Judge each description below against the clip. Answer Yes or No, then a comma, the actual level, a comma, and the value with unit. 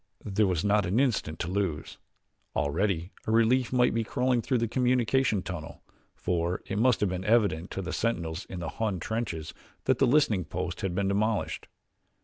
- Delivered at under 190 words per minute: Yes, average, 180 wpm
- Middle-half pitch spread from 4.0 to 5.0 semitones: Yes, average, 4.7 semitones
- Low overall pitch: Yes, low, 100 Hz